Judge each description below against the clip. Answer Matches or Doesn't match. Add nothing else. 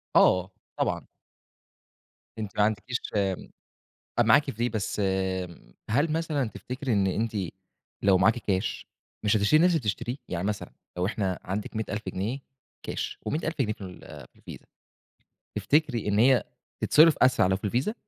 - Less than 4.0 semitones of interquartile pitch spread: Doesn't match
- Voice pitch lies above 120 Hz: Doesn't match